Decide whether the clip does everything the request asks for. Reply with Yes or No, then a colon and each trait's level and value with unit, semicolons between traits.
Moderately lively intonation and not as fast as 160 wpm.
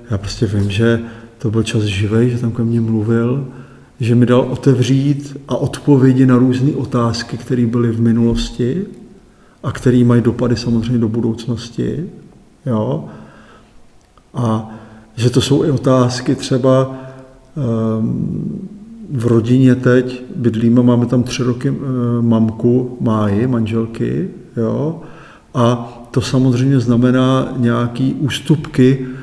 No: narrow, 2.1 semitones; average, 120 wpm